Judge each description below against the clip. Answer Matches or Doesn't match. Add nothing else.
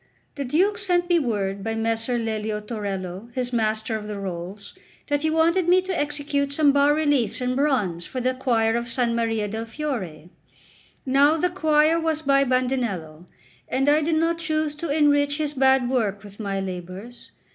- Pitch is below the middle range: Doesn't match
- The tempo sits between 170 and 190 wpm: Matches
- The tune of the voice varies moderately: Doesn't match